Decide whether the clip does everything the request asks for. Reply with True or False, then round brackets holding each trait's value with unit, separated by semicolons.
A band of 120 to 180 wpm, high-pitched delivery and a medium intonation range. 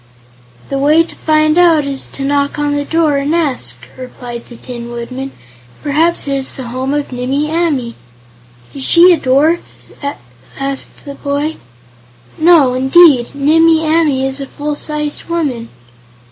True (150 wpm; 285 Hz; 3.0 semitones)